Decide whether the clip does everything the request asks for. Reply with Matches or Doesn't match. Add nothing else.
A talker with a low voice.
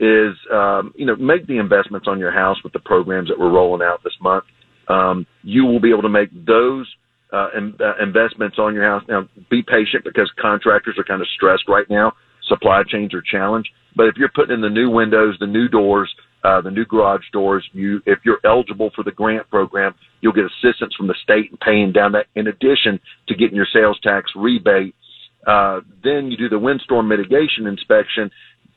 Matches